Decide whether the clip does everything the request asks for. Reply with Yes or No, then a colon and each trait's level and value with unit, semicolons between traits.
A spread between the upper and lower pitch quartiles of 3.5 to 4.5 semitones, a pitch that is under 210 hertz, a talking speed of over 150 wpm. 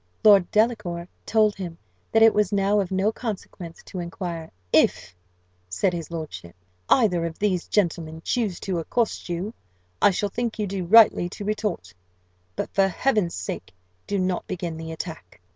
Yes: average, 3.9 semitones; medium, 185 Hz; average, 160 wpm